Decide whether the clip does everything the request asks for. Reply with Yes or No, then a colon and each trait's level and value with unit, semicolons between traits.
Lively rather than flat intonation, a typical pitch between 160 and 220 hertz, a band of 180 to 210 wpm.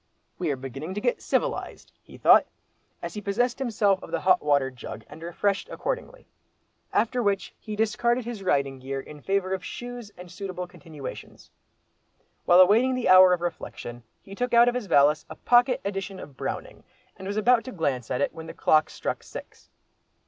Yes: wide, 7.1 semitones; high, 190 Hz; average, 185 wpm